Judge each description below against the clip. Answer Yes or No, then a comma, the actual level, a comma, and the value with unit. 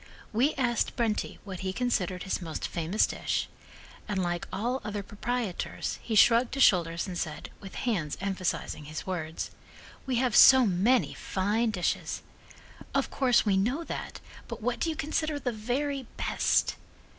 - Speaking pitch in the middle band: No, high, 210 Hz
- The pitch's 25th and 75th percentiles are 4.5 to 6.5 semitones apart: Yes, average, 5.2 semitones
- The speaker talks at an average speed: Yes, average, 155 wpm